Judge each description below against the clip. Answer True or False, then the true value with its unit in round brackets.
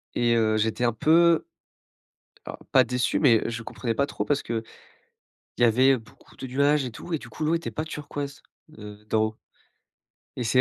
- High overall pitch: False (125 Hz)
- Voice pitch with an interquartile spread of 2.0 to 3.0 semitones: False (4.2 semitones)